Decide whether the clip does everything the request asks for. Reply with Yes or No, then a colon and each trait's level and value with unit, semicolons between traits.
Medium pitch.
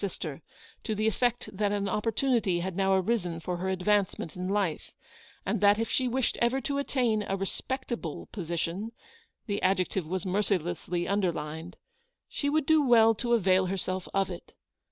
No: high, 195 Hz